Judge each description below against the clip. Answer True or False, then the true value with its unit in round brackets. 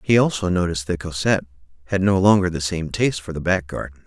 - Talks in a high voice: False (90 Hz)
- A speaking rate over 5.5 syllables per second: True (6.6 syllables/s)